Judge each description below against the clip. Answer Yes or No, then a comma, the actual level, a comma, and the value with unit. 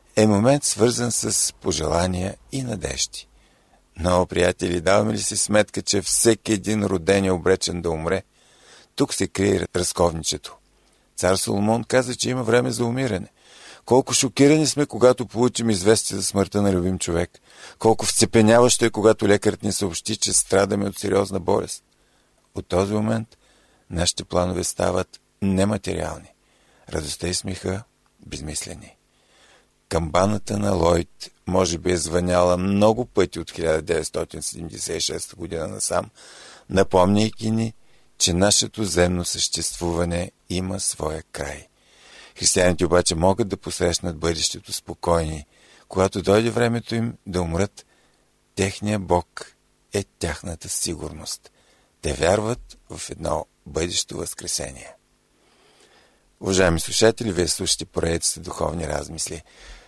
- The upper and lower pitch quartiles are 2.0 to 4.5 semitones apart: Yes, average, 3.8 semitones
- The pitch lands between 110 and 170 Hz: No, very low, 95 Hz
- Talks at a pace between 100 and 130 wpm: Yes, average, 120 wpm